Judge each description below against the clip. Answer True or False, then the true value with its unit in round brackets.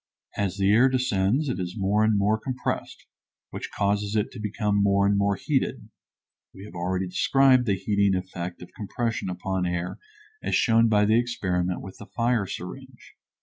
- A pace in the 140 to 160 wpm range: False (175 wpm)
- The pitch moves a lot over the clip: False (3.4 semitones)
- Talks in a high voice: False (100 Hz)